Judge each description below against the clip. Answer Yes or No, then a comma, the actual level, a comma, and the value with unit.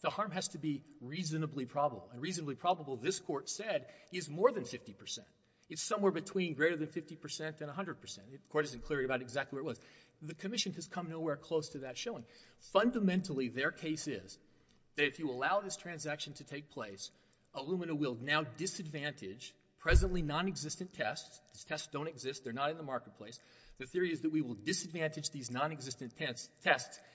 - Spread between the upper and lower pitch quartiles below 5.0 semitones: Yes, average, 4.3 semitones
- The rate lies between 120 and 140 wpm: No, average, 185 wpm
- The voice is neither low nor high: Yes, medium, 155 Hz